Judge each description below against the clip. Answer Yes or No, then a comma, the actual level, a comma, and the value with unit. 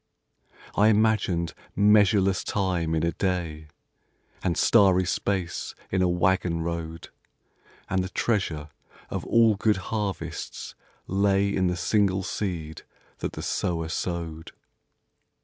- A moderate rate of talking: No, slow, 115 wpm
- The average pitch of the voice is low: Yes, very low, 95 Hz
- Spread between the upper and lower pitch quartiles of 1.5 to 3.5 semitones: Yes, average, 3.0 semitones